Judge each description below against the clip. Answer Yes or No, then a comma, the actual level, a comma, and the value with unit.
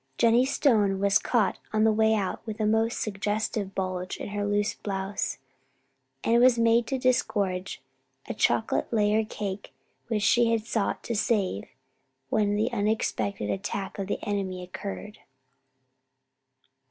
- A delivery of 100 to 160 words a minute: Yes, average, 140 wpm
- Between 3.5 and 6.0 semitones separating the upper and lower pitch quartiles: No, narrow, 2.4 semitones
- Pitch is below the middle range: No, high, 210 Hz